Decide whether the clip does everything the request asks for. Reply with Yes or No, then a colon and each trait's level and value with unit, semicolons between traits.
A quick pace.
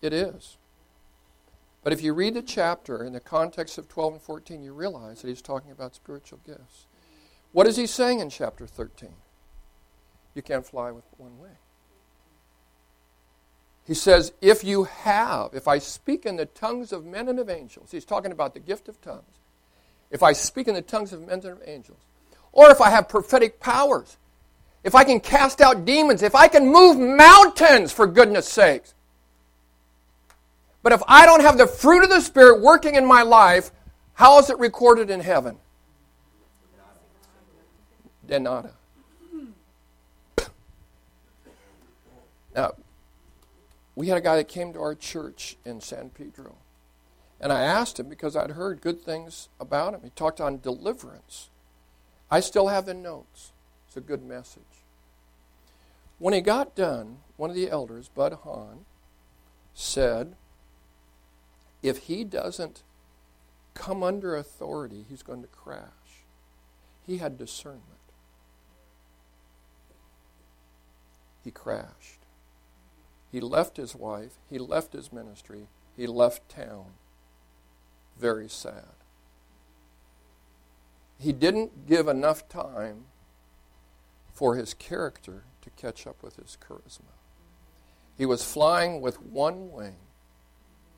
No: slow, 135 wpm